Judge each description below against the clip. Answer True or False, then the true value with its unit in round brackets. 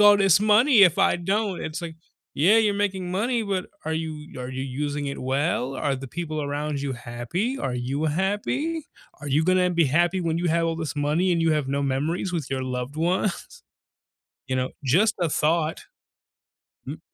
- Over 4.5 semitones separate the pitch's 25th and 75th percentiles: True (4.9 semitones)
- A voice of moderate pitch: True (160 Hz)